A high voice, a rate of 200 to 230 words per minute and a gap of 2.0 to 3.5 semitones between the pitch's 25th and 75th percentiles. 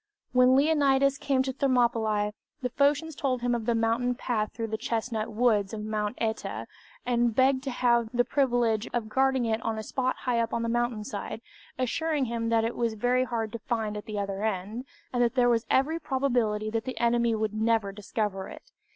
Yes: high, 235 Hz; fast, 205 wpm; average, 2.7 semitones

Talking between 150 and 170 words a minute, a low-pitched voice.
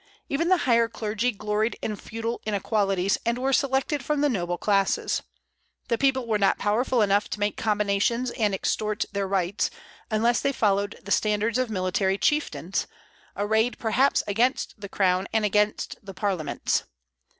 No: average, 155 wpm; high, 215 Hz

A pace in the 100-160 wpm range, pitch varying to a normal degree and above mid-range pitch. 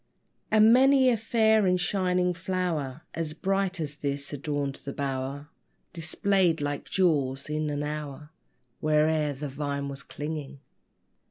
No: slow, 135 wpm; average, 4.3 semitones; medium, 155 Hz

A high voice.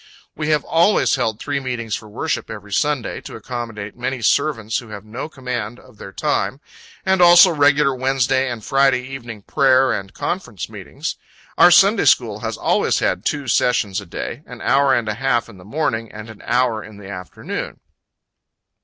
No: low, 125 Hz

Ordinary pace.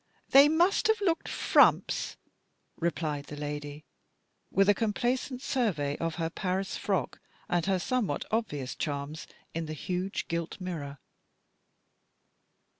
No: slow, 120 wpm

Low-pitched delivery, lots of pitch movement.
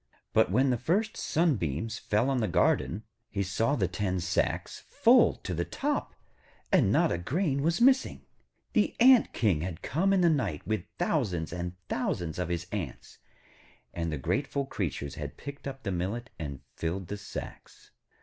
Yes: low, 105 Hz; wide, 8.3 semitones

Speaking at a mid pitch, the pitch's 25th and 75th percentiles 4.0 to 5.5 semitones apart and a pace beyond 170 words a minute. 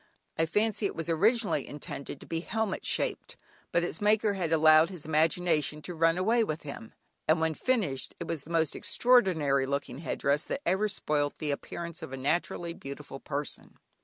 Yes: medium, 165 Hz; average, 4.4 semitones; average, 180 wpm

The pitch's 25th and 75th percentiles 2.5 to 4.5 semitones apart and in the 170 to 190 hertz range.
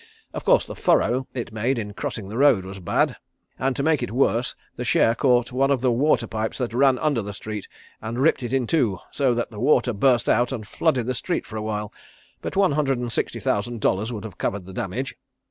No: average, 3.7 semitones; low, 120 Hz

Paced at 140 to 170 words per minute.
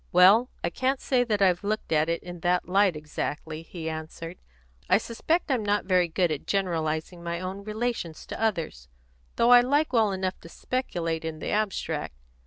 No: average, 185 wpm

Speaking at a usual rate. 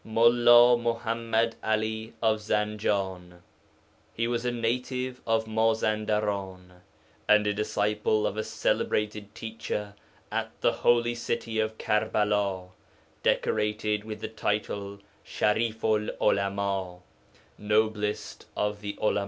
No: slow, 110 wpm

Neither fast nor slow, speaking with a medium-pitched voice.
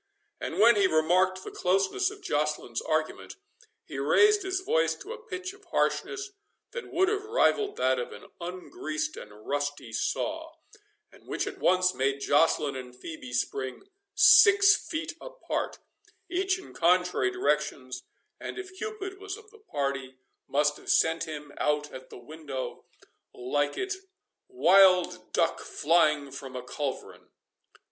Yes: average, 145 wpm; medium, 180 Hz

